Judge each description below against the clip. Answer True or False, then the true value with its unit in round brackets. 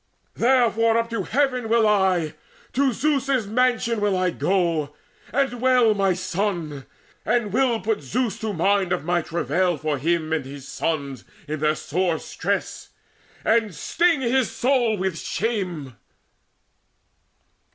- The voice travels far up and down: True (6.1 semitones)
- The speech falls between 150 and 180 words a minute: False (140 wpm)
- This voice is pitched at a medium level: False (200 Hz)